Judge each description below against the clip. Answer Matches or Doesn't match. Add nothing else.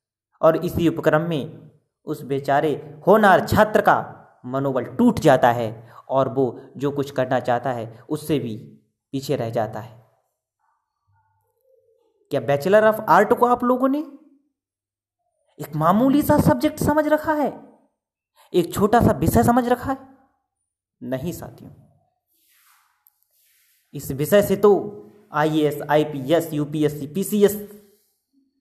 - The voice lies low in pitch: Doesn't match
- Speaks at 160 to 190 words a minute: Doesn't match